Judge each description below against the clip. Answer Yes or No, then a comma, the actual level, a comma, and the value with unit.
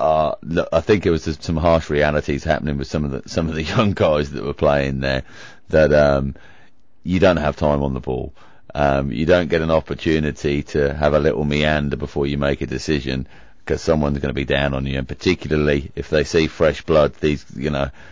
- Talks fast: Yes, fast, 220 wpm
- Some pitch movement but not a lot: No, narrow, 2.1 semitones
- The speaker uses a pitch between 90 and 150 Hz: No, very low, 75 Hz